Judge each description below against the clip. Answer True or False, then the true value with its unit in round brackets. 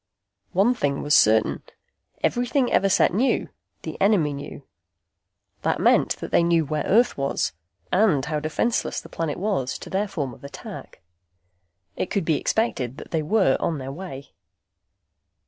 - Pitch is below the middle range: False (165 Hz)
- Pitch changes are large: True (6.3 semitones)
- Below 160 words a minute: True (145 wpm)